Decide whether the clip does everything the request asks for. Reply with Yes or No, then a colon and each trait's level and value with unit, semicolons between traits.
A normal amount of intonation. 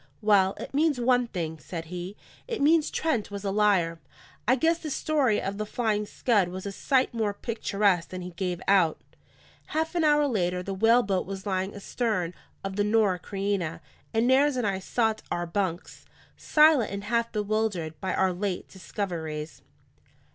Yes: average, 4.5 semitones